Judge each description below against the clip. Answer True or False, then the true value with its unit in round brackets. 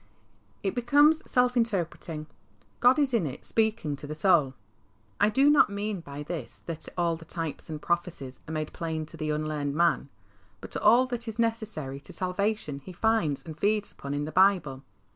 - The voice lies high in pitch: False (175 Hz)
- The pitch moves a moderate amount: False (6.4 semitones)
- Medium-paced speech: True (180 wpm)